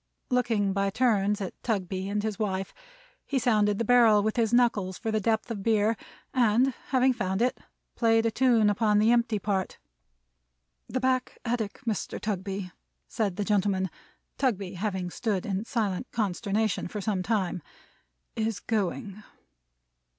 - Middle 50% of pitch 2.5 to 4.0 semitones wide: Yes, average, 2.8 semitones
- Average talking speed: Yes, average, 150 wpm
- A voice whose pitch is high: Yes, high, 215 Hz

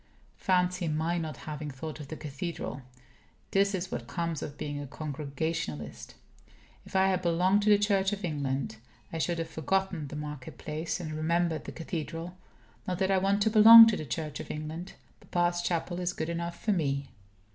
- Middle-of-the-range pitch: Yes, medium, 165 Hz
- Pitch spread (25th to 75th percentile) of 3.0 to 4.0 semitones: Yes, average, 3.4 semitones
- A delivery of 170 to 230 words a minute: Yes, average, 185 wpm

